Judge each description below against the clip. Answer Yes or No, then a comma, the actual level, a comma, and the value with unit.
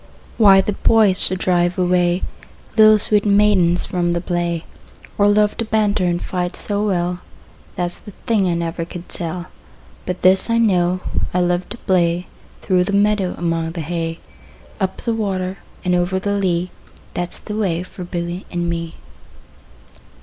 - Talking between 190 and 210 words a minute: No, average, 170 wpm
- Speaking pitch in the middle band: Yes, medium, 180 Hz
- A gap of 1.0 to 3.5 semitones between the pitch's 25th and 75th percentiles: Yes, narrow, 2.6 semitones